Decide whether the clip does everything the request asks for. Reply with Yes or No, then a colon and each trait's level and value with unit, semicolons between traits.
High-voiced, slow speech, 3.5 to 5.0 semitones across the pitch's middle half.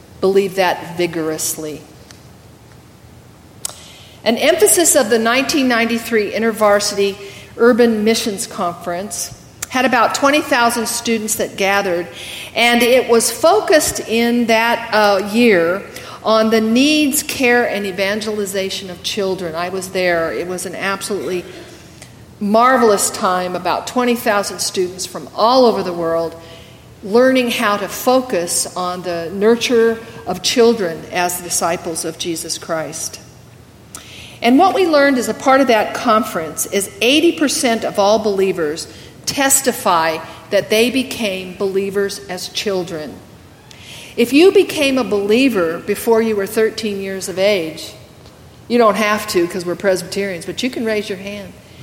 Yes: high, 205 Hz; slow, 130 wpm; average, 4.7 semitones